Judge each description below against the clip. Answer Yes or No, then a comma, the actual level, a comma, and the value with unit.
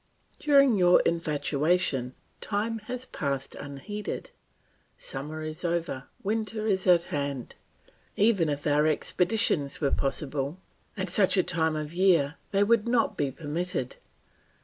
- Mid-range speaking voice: Yes, medium, 170 Hz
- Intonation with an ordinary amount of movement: No, wide, 5.8 semitones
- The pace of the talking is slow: Yes, slow, 125 wpm